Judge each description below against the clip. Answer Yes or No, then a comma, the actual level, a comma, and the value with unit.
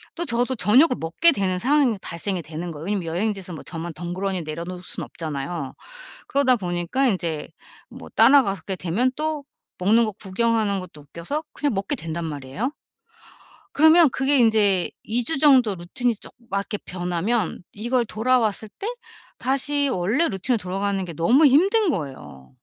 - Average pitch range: No, wide, 6.7 semitones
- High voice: Yes, high, 200 Hz